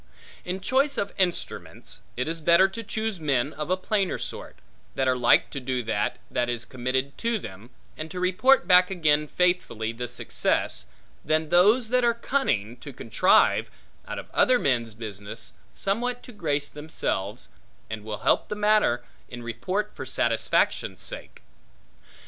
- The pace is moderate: Yes, average, 160 wpm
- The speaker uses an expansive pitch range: Yes, wide, 8.5 semitones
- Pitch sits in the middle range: Yes, medium, 155 Hz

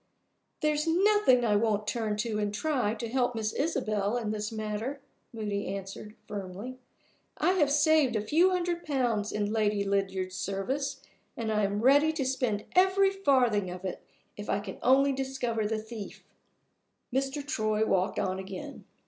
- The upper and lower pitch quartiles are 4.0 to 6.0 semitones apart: Yes, average, 5.1 semitones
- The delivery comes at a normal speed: Yes, average, 160 wpm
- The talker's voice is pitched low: No, high, 225 Hz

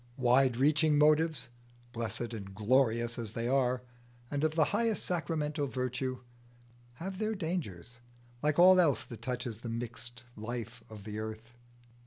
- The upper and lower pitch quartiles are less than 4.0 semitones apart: No, average, 4.6 semitones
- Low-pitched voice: Yes, low, 125 Hz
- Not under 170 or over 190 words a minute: No, average, 145 wpm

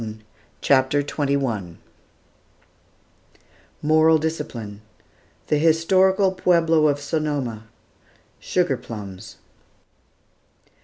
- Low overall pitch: No, medium, 145 Hz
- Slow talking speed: Yes, slow, 65 wpm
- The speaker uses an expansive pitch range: No, average, 5.0 semitones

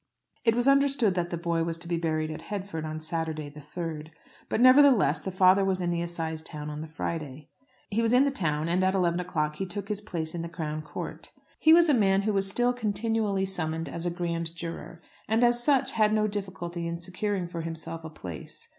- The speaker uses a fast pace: Yes, fast, 225 wpm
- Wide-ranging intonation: No, average, 4.2 semitones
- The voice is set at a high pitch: No, medium, 175 Hz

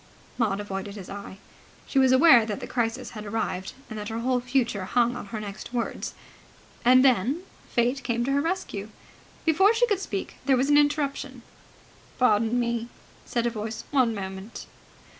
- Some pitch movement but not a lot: Yes, average, 3.9 semitones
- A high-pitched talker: Yes, high, 235 Hz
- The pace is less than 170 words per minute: No, average, 175 wpm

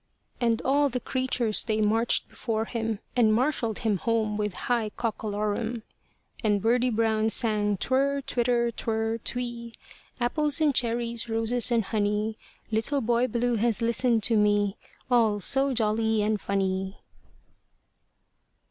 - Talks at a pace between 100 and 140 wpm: Yes, slow, 135 wpm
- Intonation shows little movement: Yes, narrow, 2.1 semitones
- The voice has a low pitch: No, high, 225 Hz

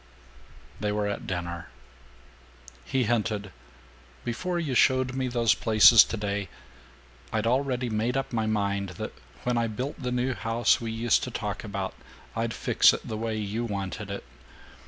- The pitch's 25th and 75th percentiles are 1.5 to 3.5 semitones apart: Yes, average, 2.9 semitones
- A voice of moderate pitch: No, low, 115 Hz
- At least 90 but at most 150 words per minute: No, average, 160 wpm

